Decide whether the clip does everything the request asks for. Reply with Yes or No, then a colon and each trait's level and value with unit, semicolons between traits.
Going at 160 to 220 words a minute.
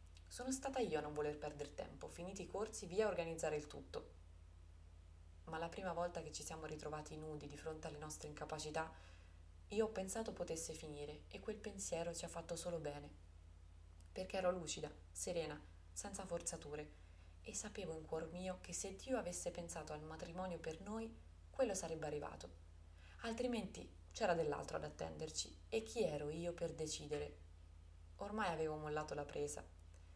Yes: average, 165 wpm